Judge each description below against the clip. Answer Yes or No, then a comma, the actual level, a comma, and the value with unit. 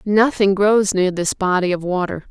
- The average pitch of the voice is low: No, high, 195 Hz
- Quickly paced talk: No, average, 180 wpm